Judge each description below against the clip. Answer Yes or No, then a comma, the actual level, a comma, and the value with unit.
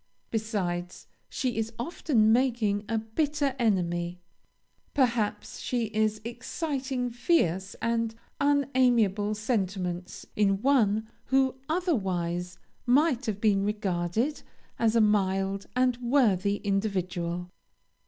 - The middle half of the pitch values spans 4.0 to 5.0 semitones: Yes, average, 4.5 semitones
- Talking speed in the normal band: No, slow, 100 wpm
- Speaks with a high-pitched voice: Yes, high, 220 Hz